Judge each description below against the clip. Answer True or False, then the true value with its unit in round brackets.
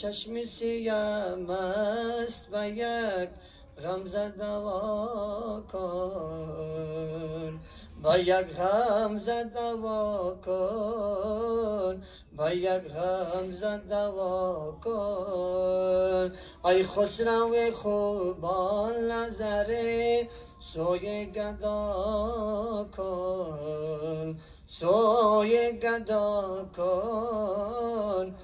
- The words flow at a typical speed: False (45 wpm)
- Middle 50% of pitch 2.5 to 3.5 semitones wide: True (2.9 semitones)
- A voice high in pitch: True (205 Hz)